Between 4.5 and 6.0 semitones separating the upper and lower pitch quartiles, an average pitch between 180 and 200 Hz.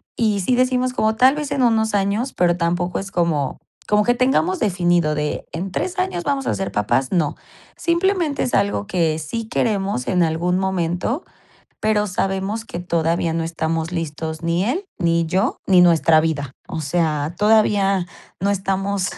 Yes: average, 4.8 semitones; high, 190 Hz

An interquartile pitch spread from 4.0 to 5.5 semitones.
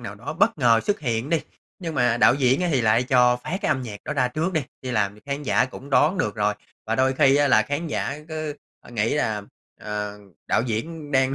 Yes: average, 4.5 semitones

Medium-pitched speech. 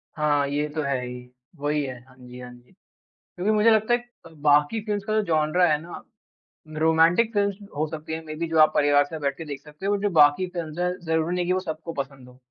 Yes: medium, 155 Hz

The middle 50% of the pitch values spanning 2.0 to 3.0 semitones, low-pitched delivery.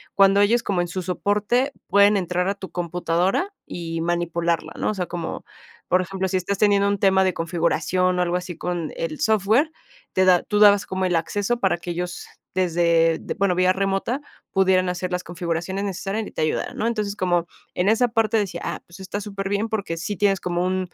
No: narrow, 2.5 semitones; medium, 185 Hz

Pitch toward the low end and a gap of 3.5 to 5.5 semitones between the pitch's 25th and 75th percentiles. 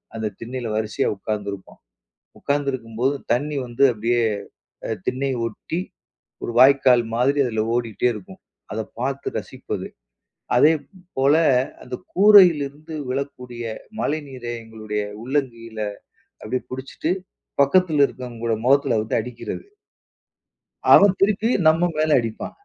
Yes: low, 125 Hz; average, 3.8 semitones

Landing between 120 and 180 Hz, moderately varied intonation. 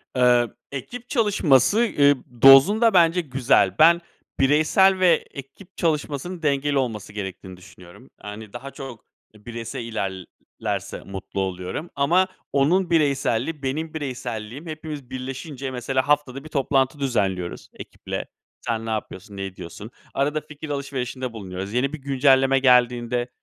Yes: low, 135 Hz; average, 4.5 semitones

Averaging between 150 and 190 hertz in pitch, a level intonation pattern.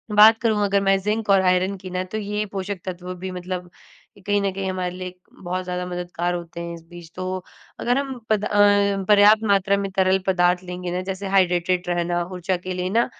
Yes: medium, 185 Hz; narrow, 2.0 semitones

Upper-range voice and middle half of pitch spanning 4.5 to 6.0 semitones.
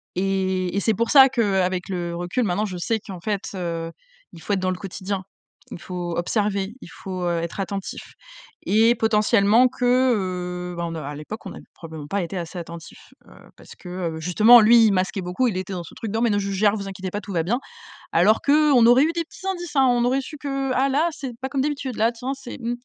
Yes: high, 200 Hz; average, 5.2 semitones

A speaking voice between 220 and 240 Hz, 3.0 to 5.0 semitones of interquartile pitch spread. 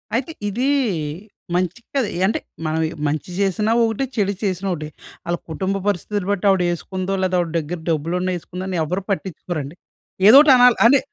No: medium, 185 Hz; average, 3.3 semitones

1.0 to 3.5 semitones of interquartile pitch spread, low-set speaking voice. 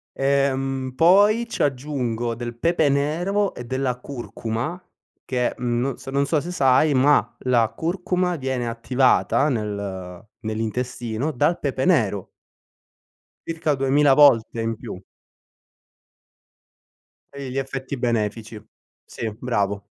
No: average, 3.9 semitones; low, 130 Hz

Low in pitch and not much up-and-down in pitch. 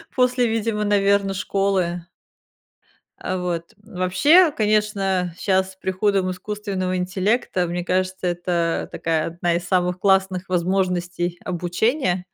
No: medium, 185 Hz; narrow, 2.2 semitones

